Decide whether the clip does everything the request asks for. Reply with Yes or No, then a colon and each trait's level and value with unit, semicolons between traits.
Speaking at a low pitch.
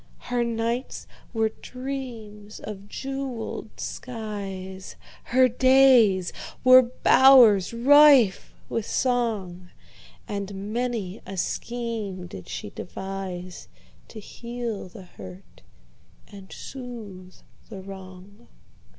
No: high, 215 Hz